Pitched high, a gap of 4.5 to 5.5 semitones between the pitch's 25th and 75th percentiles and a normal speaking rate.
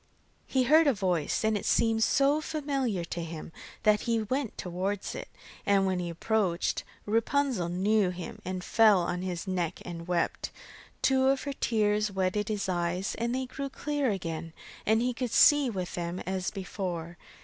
Yes: high, 205 Hz; average, 5.2 semitones; average, 170 wpm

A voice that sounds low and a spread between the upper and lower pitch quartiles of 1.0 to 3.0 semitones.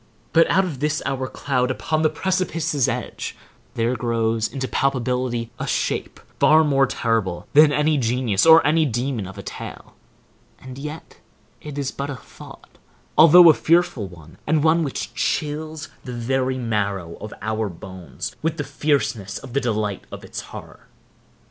No: low, 130 Hz; average, 5.1 semitones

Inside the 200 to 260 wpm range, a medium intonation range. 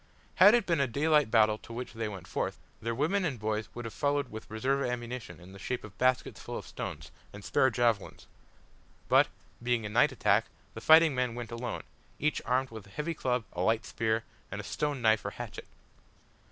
Yes: fast, 205 wpm; average, 4.0 semitones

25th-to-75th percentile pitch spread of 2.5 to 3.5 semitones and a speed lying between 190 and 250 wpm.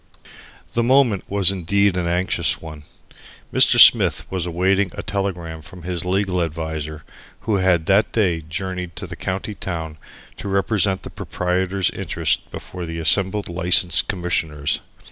No: average, 2.9 semitones; average, 145 wpm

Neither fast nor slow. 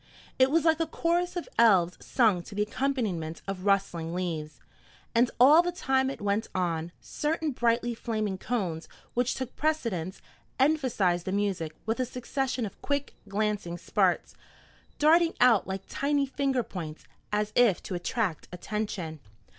Yes: average, 150 wpm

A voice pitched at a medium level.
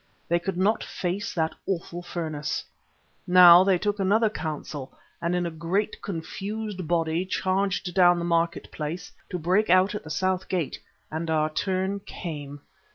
Yes: medium, 175 Hz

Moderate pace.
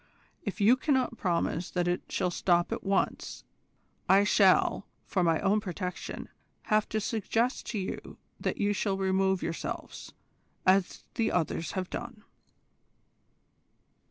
No: slow, 130 wpm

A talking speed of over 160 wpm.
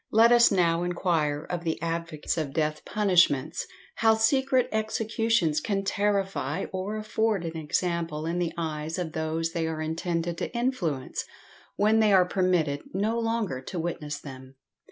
No: average, 155 wpm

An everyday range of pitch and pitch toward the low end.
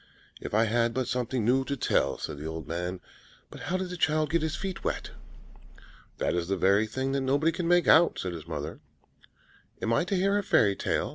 No: wide, 9.0 semitones; low, 125 Hz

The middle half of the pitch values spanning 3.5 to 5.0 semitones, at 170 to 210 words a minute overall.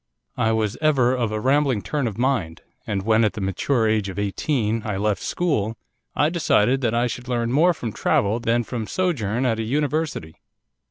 Yes: average, 4.1 semitones; average, 195 wpm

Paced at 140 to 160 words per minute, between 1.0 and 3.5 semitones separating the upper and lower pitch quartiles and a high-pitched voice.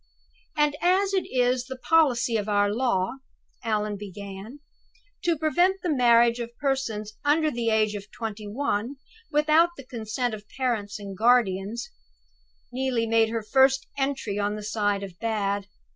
No: average, 150 wpm; average, 4.4 semitones; high, 230 Hz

